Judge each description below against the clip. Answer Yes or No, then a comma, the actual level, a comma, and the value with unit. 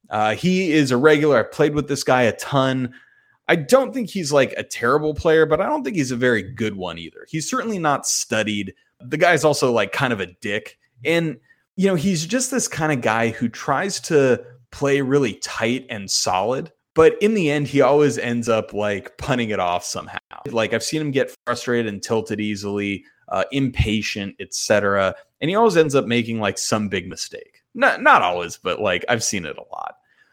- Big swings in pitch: Yes, wide, 6.3 semitones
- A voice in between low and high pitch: No, low, 130 Hz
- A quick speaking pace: Yes, fast, 210 wpm